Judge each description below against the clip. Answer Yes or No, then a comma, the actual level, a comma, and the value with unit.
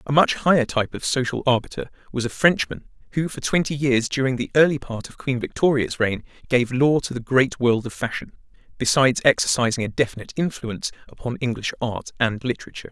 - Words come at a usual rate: Yes, average, 185 wpm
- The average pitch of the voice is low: Yes, low, 130 Hz